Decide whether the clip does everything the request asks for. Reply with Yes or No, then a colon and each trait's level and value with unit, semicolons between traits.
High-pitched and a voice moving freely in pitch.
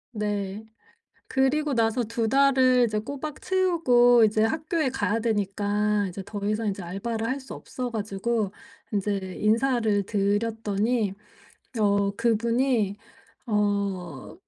No: high, 220 Hz; average, 3.4 semitones